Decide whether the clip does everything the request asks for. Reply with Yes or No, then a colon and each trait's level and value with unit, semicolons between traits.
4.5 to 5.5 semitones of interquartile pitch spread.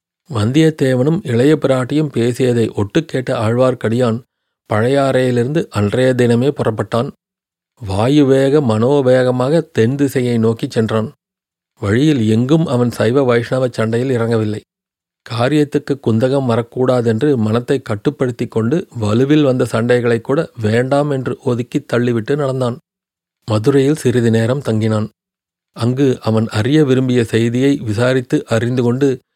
No: average, 3.6 semitones